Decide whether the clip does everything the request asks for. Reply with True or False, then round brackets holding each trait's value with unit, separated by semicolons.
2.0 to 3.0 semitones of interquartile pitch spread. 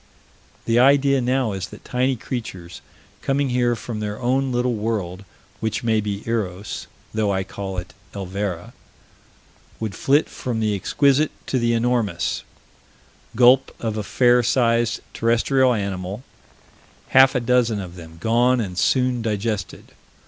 False (3.8 semitones)